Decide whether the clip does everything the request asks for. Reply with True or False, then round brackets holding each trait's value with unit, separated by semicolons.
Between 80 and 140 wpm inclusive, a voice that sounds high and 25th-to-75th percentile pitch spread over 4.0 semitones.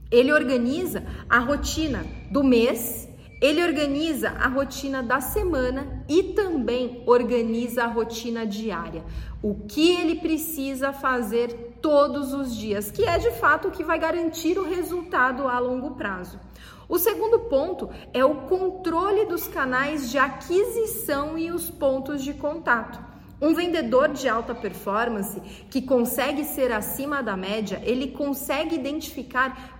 True (135 wpm; 275 Hz; 4.8 semitones)